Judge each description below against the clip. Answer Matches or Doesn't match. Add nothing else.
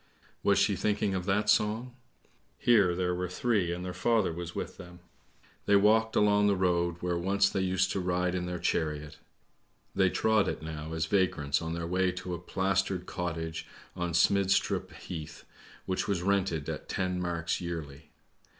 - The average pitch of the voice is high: Doesn't match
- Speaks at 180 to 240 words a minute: Doesn't match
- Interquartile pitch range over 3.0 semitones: Doesn't match